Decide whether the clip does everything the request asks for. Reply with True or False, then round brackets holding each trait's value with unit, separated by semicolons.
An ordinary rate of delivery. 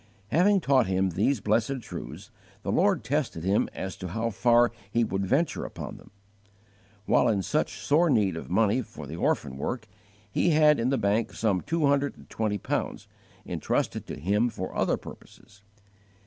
True (175 wpm)